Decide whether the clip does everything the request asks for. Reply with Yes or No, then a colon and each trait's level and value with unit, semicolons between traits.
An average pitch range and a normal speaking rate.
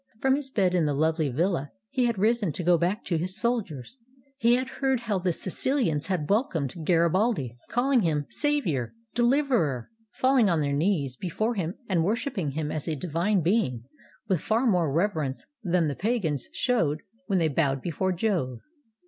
No: wide, 6.9 semitones; average, 175 wpm